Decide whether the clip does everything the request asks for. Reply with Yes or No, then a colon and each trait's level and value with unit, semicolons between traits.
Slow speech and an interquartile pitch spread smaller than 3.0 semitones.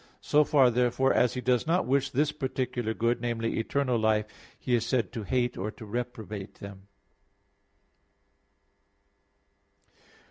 Yes: slow, 130 wpm; narrow, 2.6 semitones